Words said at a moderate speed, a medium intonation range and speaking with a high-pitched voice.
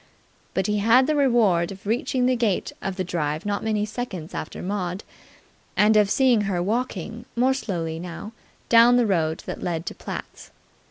Yes: average, 175 wpm; average, 4.9 semitones; high, 205 Hz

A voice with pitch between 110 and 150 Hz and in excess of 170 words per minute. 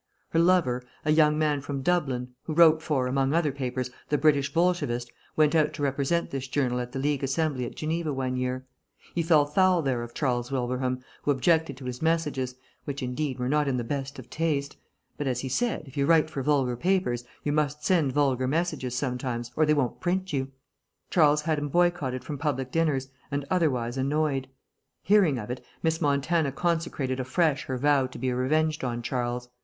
Yes: medium, 140 Hz; average, 195 wpm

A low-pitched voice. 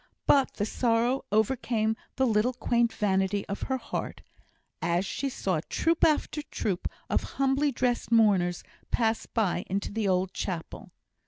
No: high, 220 Hz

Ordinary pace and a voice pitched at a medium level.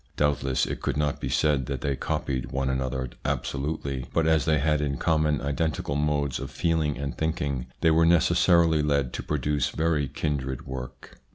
No: average, 175 wpm; very low, 70 Hz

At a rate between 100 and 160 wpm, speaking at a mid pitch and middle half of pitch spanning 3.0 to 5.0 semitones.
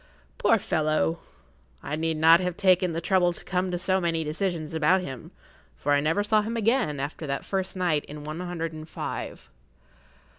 No: average, 185 wpm; medium, 165 Hz; average, 3.3 semitones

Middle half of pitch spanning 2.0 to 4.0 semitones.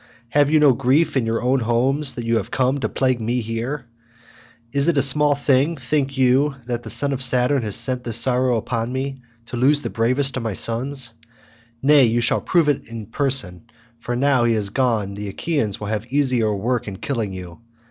Yes: average, 3.3 semitones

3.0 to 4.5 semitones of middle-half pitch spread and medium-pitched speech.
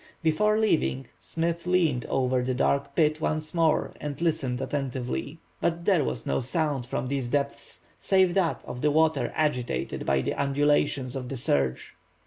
Yes: average, 4.1 semitones; medium, 145 Hz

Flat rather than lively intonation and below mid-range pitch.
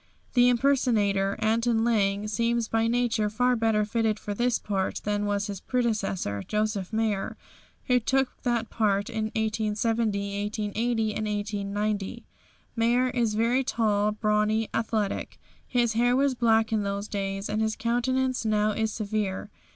No: narrow, 2.2 semitones; high, 220 Hz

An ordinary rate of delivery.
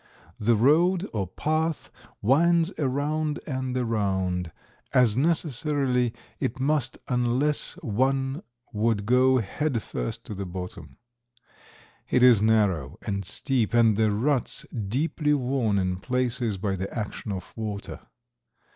No: slow, 120 wpm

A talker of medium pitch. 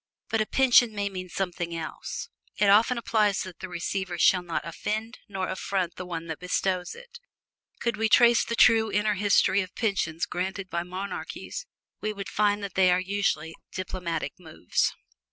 No: high, 195 Hz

